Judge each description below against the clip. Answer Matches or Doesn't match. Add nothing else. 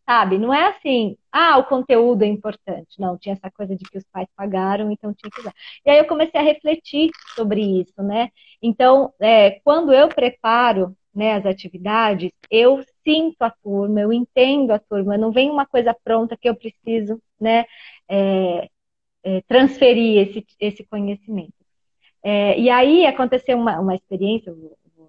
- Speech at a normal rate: Matches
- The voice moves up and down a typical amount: Matches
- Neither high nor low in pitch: Doesn't match